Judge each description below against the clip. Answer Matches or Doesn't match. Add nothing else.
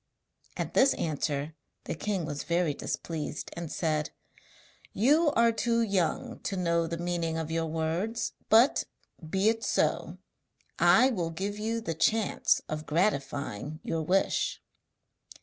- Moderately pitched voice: Matches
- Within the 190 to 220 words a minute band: Doesn't match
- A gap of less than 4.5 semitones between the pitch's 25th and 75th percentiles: Doesn't match